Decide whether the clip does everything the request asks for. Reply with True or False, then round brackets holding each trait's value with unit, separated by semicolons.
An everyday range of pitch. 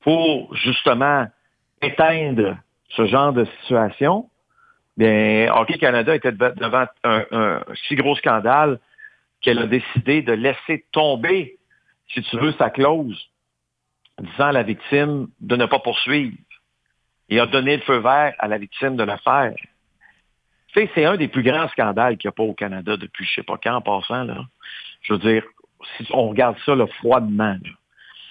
True (4.7 semitones)